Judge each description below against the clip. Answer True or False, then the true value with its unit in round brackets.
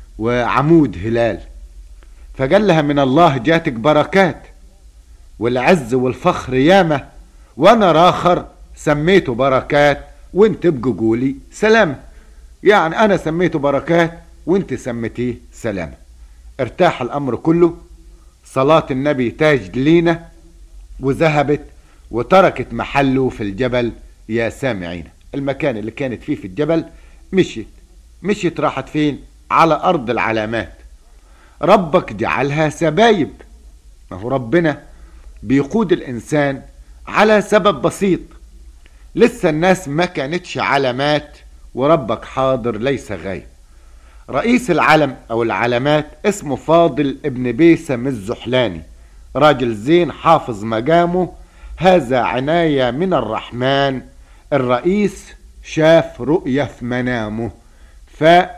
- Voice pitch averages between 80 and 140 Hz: True (135 Hz)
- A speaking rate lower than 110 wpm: True (100 wpm)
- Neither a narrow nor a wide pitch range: False (6.7 semitones)